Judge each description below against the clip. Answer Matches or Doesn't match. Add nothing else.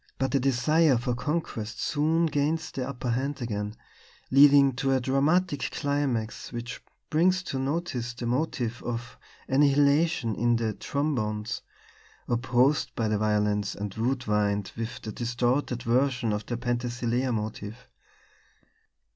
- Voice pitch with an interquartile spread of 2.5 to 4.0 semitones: Matches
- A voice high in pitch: Doesn't match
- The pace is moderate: Doesn't match